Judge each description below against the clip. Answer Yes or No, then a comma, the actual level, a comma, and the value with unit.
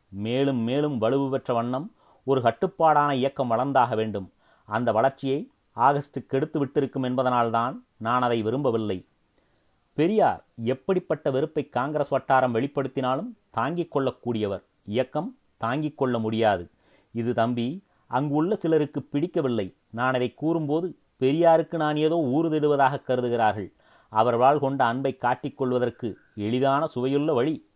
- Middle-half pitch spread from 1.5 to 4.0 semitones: Yes, average, 3.7 semitones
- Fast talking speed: No, average, 115 wpm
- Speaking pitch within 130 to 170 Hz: Yes, low, 135 Hz